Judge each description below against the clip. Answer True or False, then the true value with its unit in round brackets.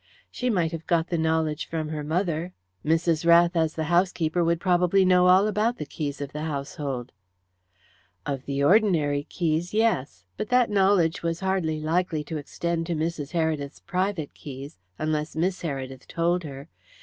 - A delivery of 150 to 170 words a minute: True (165 wpm)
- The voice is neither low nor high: True (165 Hz)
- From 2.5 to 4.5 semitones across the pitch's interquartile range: True (3.0 semitones)